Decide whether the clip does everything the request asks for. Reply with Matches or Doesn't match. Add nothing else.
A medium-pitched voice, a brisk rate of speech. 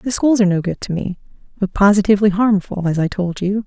Doesn't match